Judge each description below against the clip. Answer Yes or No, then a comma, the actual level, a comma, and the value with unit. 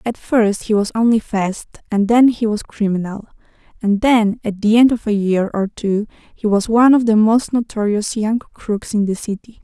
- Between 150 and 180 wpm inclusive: No, fast, 205 wpm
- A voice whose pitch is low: No, high, 215 Hz